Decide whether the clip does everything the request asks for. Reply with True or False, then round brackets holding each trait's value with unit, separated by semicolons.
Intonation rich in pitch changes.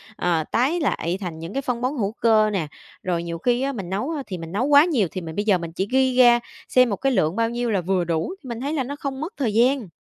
True (6.3 semitones)